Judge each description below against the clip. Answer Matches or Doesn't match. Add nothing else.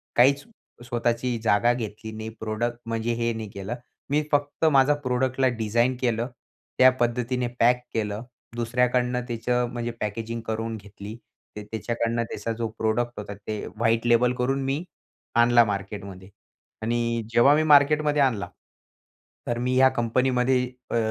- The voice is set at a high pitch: Doesn't match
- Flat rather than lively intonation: Matches